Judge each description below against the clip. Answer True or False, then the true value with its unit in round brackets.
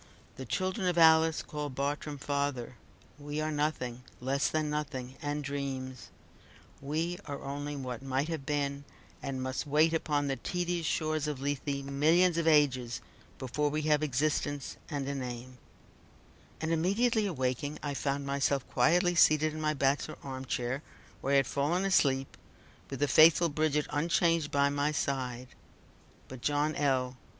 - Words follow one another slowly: False (155 wpm)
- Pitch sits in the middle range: True (145 Hz)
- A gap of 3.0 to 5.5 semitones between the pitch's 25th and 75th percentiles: False (2.4 semitones)